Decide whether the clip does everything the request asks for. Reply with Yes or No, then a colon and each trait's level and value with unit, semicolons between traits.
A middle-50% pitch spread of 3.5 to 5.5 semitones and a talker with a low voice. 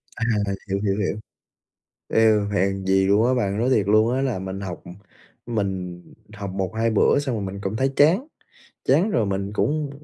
Yes: average, 4.1 semitones; low, 105 Hz